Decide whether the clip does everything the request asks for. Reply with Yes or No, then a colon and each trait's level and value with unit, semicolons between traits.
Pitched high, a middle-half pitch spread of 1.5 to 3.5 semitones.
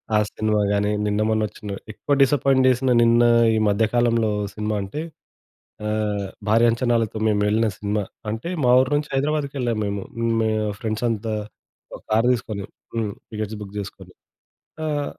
No: low, 110 Hz; narrow, 2.6 semitones